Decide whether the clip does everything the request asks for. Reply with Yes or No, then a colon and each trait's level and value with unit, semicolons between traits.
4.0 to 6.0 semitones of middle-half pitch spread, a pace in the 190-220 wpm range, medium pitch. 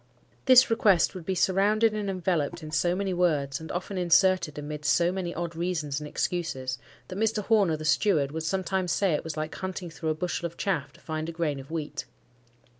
No: average, 3.6 semitones; fast, 205 wpm; medium, 170 Hz